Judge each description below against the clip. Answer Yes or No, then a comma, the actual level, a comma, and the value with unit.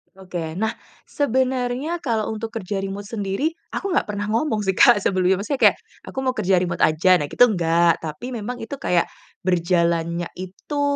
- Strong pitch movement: Yes, wide, 5.7 semitones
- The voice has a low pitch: No, high, 200 Hz